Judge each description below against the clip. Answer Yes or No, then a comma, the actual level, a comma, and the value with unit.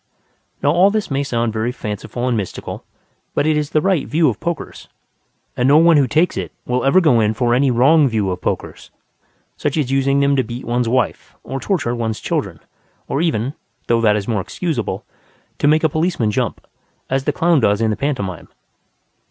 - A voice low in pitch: Yes, low, 130 Hz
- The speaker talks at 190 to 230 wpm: Yes, average, 200 wpm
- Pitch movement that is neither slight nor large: Yes, average, 5.0 semitones